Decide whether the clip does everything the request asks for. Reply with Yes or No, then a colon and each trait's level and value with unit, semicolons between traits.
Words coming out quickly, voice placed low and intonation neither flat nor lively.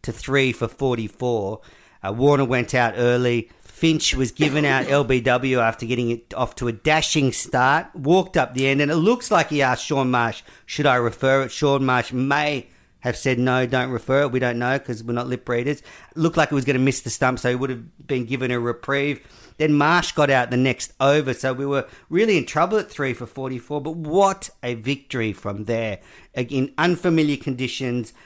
Yes: fast, 210 wpm; low, 130 Hz; average, 3.1 semitones